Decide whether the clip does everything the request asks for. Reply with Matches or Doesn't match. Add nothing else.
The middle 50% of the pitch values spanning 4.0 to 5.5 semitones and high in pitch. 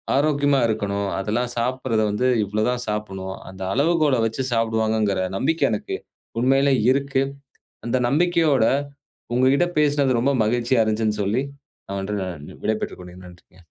Doesn't match